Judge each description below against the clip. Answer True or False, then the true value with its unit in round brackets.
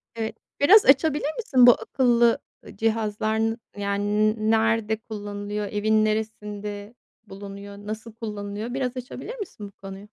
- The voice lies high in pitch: True (220 Hz)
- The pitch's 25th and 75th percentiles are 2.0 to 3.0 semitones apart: True (2.5 semitones)